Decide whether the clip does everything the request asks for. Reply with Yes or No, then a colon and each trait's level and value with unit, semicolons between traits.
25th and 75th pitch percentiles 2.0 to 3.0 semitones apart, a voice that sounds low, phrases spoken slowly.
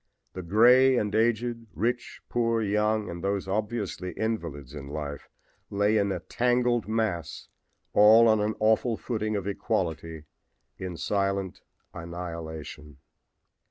No: average, 4.6 semitones; low, 105 Hz; slow, 125 wpm